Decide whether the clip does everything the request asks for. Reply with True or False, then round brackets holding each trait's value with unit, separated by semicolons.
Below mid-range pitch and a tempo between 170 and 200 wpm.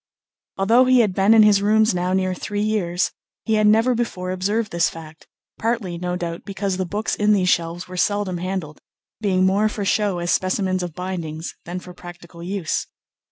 False (185 Hz; 190 wpm)